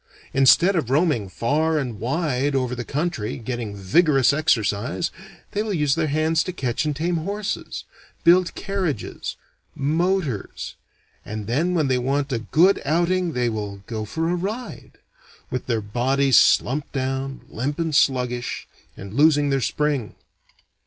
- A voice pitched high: No, medium, 140 Hz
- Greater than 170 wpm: No, average, 145 wpm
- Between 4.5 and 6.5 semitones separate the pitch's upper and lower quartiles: Yes, average, 5.1 semitones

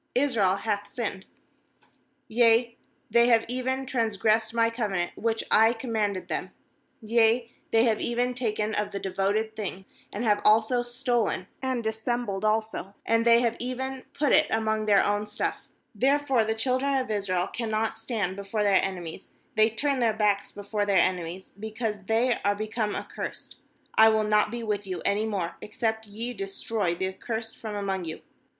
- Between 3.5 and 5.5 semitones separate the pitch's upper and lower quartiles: No, narrow, 2.6 semitones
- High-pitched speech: Yes, high, 220 Hz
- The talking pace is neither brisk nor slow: Yes, average, 170 wpm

